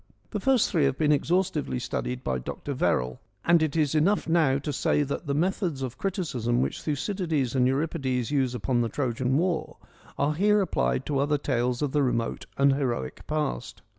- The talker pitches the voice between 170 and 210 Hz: No, medium, 140 Hz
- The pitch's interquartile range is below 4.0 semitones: No, average, 4.3 semitones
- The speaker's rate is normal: Yes, average, 185 wpm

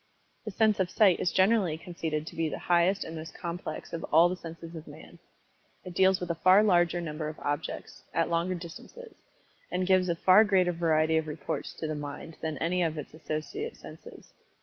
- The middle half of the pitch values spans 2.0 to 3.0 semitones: Yes, narrow, 2.5 semitones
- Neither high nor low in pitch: Yes, medium, 170 Hz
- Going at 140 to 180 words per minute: No, average, 200 wpm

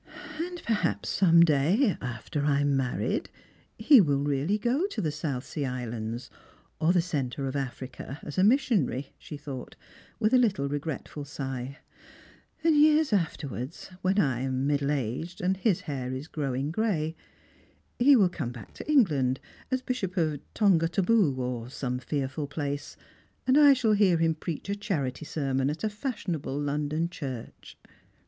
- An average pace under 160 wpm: No, average, 165 wpm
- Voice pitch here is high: No, medium, 150 Hz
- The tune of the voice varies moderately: No, wide, 6.8 semitones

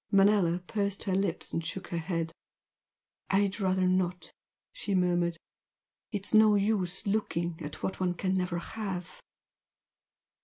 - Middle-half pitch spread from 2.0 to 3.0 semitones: Yes, narrow, 2.4 semitones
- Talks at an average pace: No, slow, 130 wpm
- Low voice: No, medium, 185 Hz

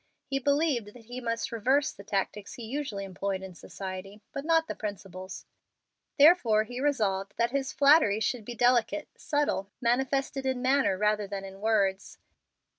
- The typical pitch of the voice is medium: No, high, 230 Hz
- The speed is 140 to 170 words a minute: Yes, average, 160 wpm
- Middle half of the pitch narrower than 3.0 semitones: No, wide, 5.4 semitones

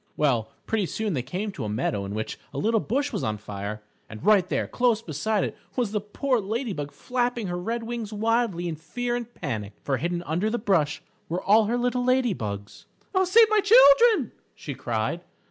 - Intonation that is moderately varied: No, wide, 8.6 semitones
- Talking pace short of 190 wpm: No, fast, 205 wpm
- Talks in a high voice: Yes, high, 205 Hz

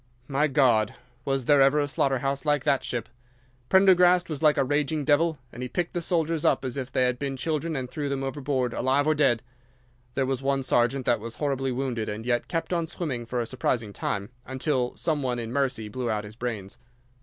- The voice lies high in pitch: No, low, 135 Hz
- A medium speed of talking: No, fast, 215 wpm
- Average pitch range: Yes, average, 3.3 semitones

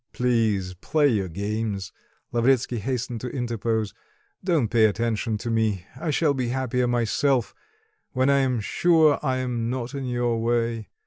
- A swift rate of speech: No, average, 150 wpm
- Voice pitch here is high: No, low, 120 Hz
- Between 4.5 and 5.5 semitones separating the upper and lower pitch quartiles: No, average, 2.7 semitones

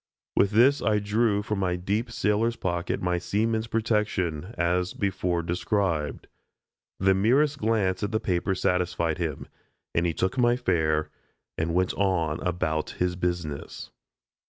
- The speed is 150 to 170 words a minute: No, average, 140 wpm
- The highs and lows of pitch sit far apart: No, average, 3.6 semitones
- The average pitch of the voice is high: No, very low, 95 Hz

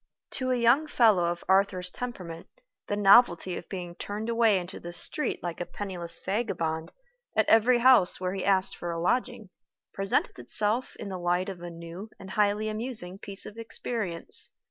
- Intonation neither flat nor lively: Yes, average, 4.2 semitones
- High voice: Yes, high, 195 Hz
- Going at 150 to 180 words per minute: Yes, average, 175 wpm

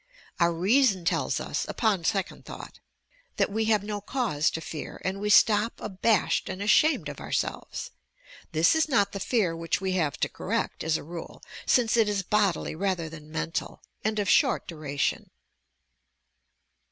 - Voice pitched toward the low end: No, high, 195 Hz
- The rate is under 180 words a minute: Yes, average, 165 wpm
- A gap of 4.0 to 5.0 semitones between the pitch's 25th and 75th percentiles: Yes, average, 4.5 semitones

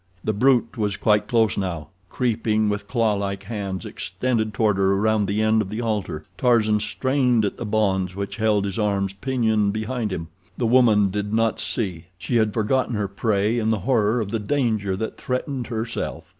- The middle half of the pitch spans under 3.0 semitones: Yes, narrow, 2.5 semitones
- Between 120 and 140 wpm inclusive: No, average, 175 wpm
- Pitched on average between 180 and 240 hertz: No, low, 110 Hz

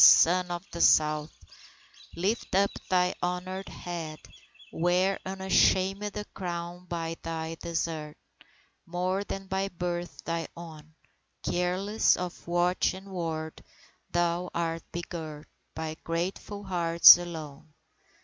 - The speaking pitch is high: No, medium, 175 Hz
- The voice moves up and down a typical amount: No, narrow, 2.1 semitones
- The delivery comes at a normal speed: No, slow, 110 wpm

